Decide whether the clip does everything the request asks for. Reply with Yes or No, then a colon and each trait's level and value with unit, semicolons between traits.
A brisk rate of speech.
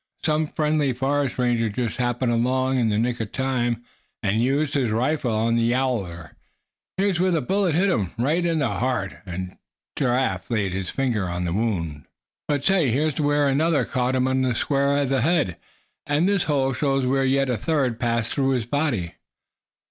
No: average, 180 wpm